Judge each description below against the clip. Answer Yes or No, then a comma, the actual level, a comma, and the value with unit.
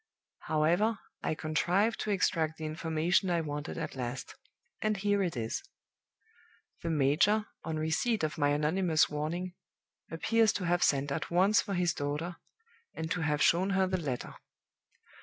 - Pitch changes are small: No, average, 3.7 semitones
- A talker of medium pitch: Yes, medium, 165 Hz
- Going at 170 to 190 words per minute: No, average, 155 wpm